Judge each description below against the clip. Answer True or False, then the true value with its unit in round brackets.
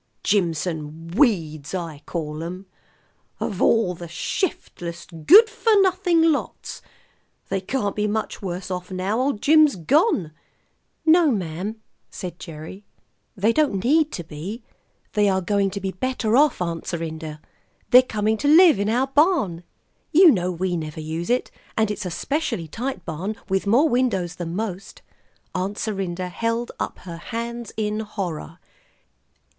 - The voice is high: True (200 Hz)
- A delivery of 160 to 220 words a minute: False (150 wpm)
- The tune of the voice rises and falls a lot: True (6.0 semitones)